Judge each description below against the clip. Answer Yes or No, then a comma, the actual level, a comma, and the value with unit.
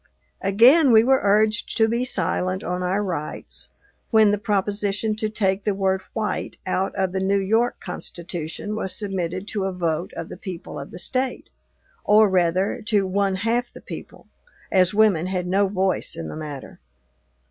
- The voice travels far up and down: No, average, 2.7 semitones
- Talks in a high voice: Yes, high, 195 Hz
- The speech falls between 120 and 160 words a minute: No, average, 170 wpm